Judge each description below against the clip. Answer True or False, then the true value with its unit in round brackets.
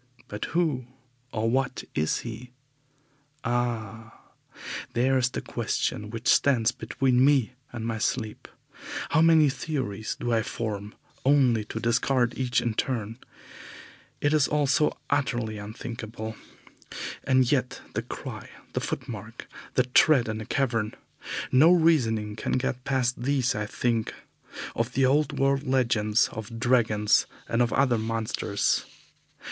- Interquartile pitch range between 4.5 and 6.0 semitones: False (3.2 semitones)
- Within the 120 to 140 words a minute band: True (135 wpm)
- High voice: False (120 Hz)